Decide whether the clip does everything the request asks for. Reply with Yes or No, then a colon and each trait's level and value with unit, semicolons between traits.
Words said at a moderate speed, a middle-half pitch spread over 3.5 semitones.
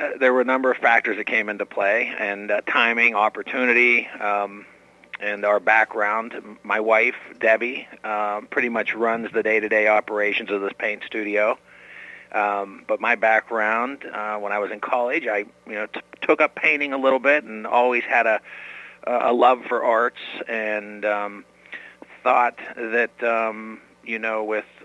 No: average, 165 wpm; narrow, 2.4 semitones